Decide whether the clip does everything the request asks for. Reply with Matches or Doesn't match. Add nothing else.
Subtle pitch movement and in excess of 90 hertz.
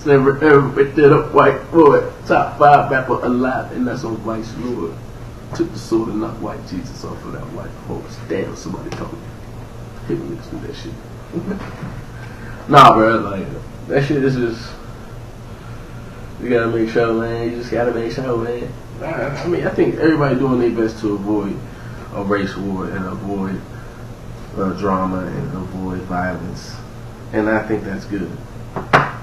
Matches